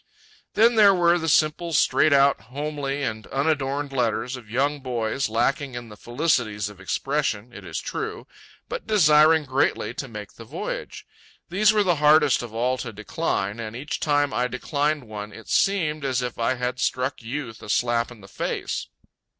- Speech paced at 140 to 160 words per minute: No, average, 175 wpm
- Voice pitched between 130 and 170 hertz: Yes, low, 135 Hz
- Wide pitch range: No, average, 4.6 semitones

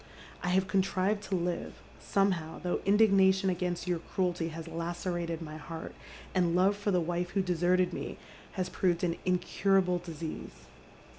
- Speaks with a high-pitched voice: No, medium, 180 Hz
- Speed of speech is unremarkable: Yes, average, 150 wpm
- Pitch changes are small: Yes, narrow, 2.0 semitones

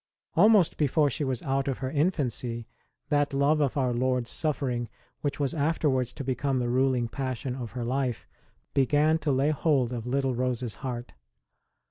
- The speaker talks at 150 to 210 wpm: Yes, average, 175 wpm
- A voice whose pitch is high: No, low, 135 Hz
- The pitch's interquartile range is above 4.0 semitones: No, average, 2.7 semitones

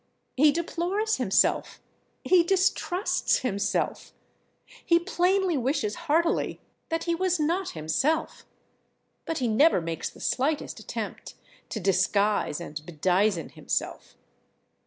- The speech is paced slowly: Yes, slow, 110 wpm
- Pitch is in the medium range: No, very high, 305 Hz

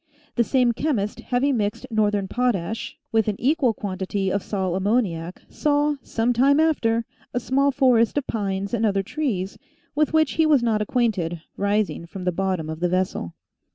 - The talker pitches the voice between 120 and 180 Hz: No, high, 220 Hz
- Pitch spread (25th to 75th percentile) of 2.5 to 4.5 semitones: No, average, 5.0 semitones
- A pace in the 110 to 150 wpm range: No, average, 170 wpm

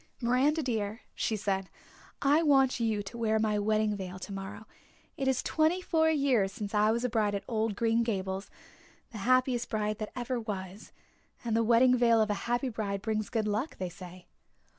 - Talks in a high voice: Yes, high, 220 Hz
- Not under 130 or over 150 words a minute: No, average, 185 wpm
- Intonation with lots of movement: No, average, 3.3 semitones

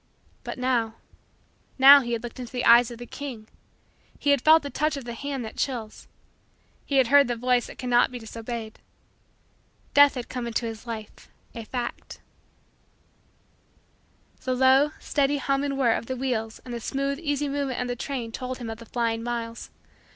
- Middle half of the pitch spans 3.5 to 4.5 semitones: No, average, 2.9 semitones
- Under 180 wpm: No, average, 185 wpm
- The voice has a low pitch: No, high, 245 Hz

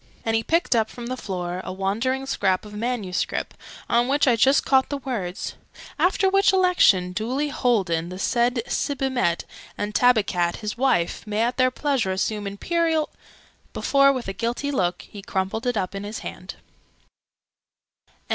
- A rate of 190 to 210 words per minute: No, average, 165 wpm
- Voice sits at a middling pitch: No, high, 230 Hz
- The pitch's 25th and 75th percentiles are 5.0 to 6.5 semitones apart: Yes, wide, 5.4 semitones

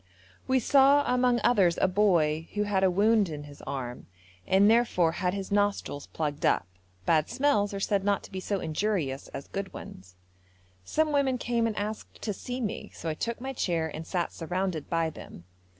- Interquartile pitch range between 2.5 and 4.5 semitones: No, wide, 5.6 semitones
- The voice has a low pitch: No, high, 195 Hz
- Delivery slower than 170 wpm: No, average, 190 wpm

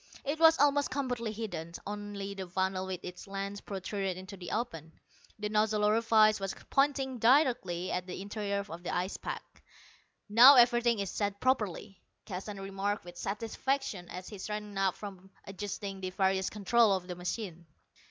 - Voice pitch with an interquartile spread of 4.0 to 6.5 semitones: No, average, 3.1 semitones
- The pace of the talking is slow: No, average, 160 wpm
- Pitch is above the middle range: Yes, high, 200 Hz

